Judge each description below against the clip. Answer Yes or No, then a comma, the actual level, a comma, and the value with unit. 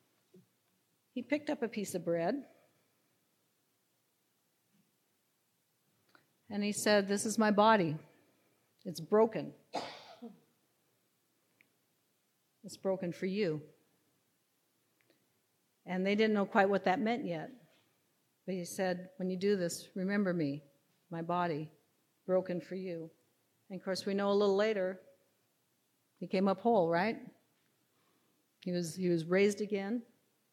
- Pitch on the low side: No, high, 190 Hz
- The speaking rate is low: Yes, slow, 120 wpm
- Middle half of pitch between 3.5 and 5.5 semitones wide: No, average, 3.1 semitones